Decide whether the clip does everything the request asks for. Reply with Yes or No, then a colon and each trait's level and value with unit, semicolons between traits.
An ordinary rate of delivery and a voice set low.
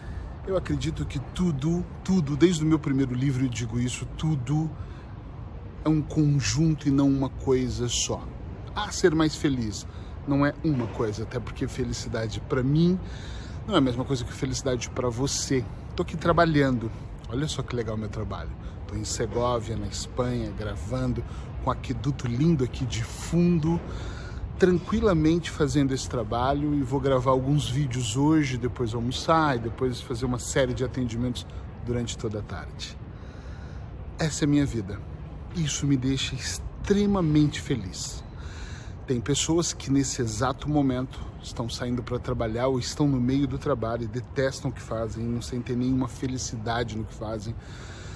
Yes: average, 160 wpm; low, 125 Hz